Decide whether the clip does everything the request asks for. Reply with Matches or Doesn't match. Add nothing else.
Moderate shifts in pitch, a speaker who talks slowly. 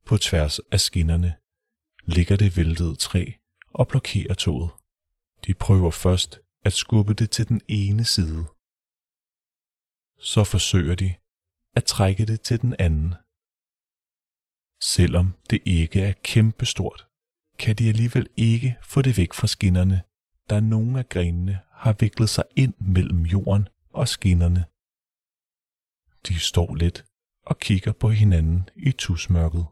Matches